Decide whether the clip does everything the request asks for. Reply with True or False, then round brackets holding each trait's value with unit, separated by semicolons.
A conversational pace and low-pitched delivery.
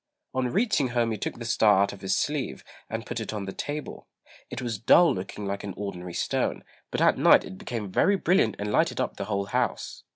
False (225 wpm; 110 Hz)